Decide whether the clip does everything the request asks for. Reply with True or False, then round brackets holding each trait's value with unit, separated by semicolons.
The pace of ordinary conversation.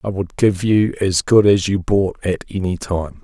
False (220 wpm)